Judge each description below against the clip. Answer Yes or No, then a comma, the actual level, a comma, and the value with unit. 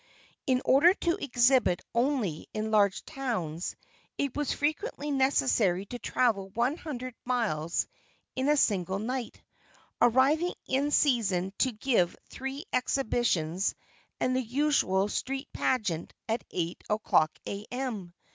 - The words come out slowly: Yes, slow, 120 wpm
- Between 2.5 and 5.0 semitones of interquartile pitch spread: No, wide, 5.6 semitones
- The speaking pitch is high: Yes, high, 245 Hz